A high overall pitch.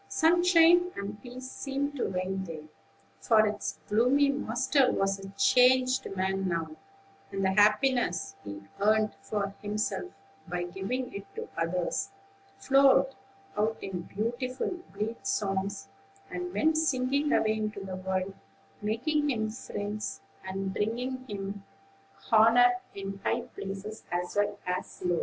Yes: high, 215 Hz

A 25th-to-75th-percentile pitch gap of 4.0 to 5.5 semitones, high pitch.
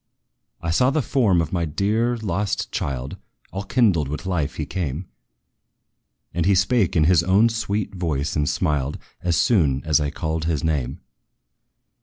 No: average, 4.8 semitones; very low, 85 Hz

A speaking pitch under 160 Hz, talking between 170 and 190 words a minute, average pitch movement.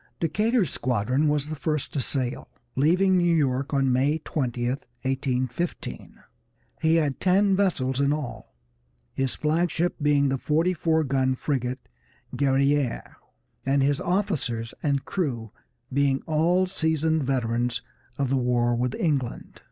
No: medium, 140 Hz; slow, 135 wpm; average, 3.7 semitones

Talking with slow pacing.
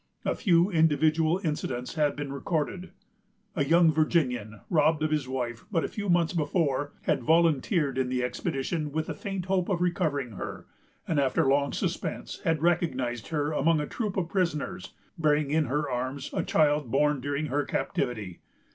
No: average, 170 wpm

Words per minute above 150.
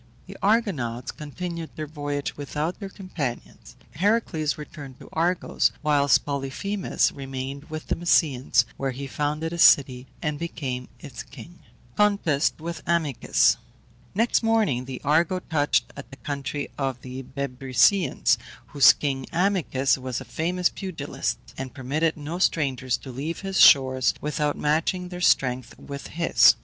No: average, 140 wpm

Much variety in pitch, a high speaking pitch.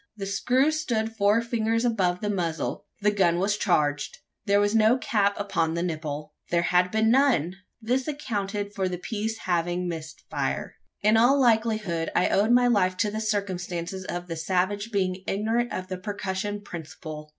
No: average, 3.8 semitones; high, 200 Hz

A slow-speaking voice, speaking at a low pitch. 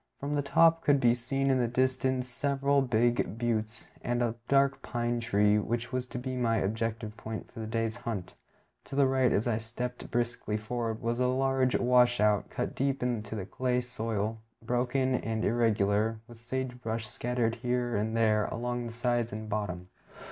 No: average, 180 wpm; low, 120 Hz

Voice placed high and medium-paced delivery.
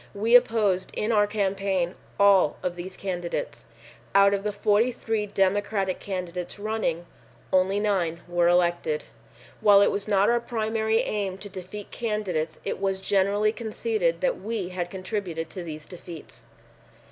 Yes: high, 200 Hz; average, 145 wpm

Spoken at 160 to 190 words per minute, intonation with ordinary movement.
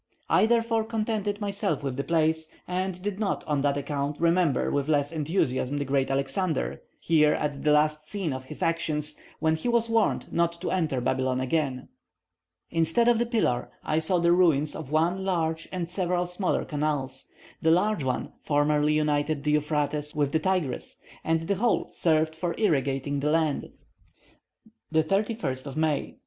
Yes: average, 165 wpm; average, 3.9 semitones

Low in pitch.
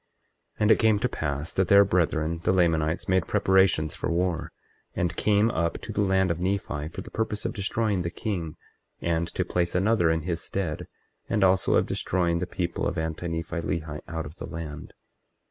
Yes: very low, 85 Hz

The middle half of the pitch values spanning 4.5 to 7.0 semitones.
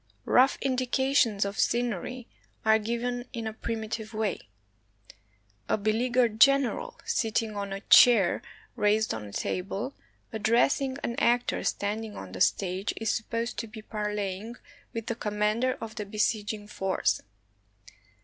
No: narrow, 2.5 semitones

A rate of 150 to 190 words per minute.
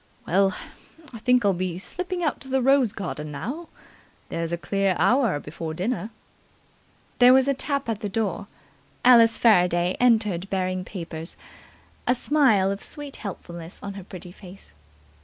Yes: average, 160 wpm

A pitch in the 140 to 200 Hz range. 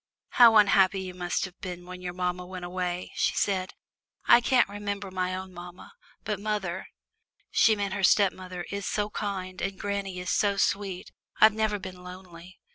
Yes: high, 190 Hz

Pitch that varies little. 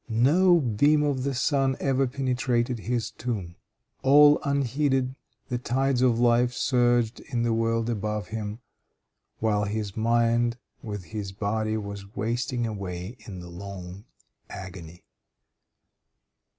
No: average, 3.7 semitones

